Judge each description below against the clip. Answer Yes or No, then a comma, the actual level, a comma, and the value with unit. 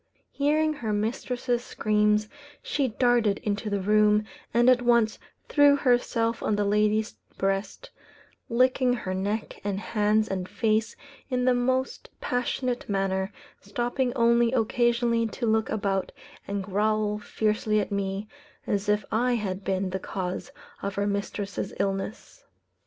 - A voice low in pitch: No, high, 215 Hz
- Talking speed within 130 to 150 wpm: Yes, slow, 135 wpm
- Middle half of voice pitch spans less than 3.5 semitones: Yes, average, 3.1 semitones